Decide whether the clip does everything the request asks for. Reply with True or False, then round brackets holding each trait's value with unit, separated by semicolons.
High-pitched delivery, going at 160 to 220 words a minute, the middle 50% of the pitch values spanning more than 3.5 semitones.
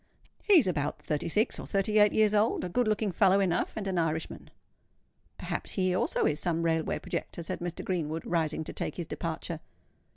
False (175 Hz; 195 wpm; 3.9 semitones)